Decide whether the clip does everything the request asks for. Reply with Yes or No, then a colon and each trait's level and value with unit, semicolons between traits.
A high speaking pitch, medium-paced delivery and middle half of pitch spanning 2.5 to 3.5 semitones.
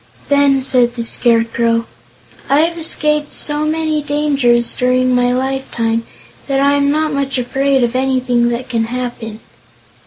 Yes: very high, 260 Hz; average, 145 wpm; average, 3.1 semitones